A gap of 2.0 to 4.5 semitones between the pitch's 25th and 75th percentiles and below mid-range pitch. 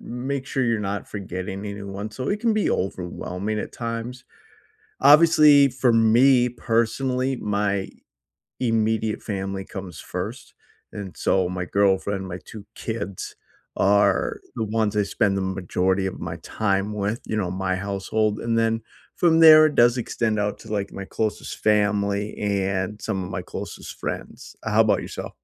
Yes: average, 3.1 semitones; low, 105 Hz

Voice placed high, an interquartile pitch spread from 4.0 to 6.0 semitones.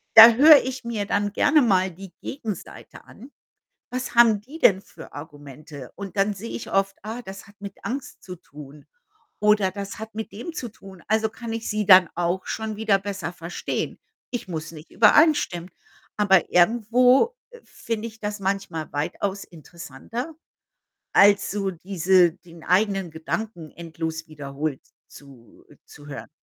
Yes: high, 195 Hz; average, 4.6 semitones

